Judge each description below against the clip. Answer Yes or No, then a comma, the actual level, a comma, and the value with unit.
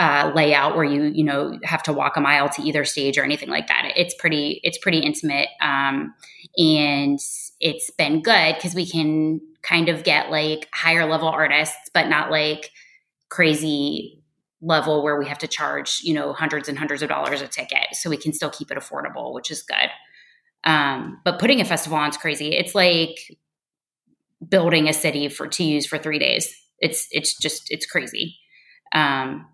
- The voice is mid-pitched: Yes, medium, 155 Hz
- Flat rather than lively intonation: Yes, narrow, 1.8 semitones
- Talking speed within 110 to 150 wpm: No, average, 185 wpm